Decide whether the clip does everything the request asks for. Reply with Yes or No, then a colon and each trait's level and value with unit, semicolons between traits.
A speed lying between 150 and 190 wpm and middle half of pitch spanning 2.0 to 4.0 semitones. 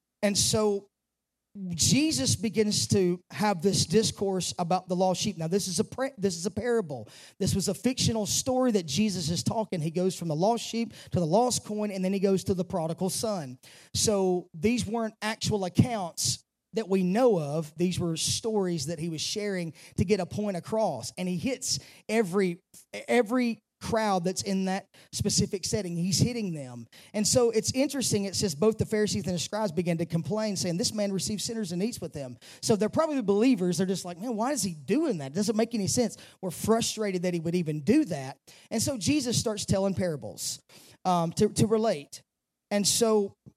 No: average, 200 wpm; average, 3.7 semitones